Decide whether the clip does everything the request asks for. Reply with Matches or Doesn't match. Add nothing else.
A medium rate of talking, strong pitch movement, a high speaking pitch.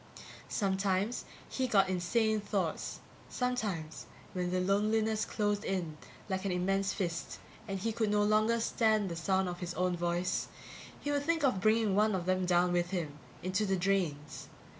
Doesn't match